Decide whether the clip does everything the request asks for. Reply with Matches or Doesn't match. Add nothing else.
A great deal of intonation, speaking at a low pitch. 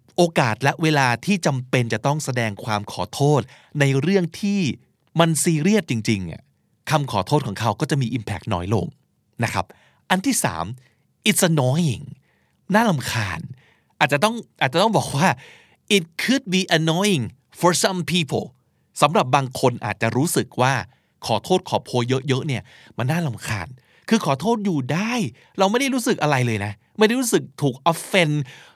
Doesn't match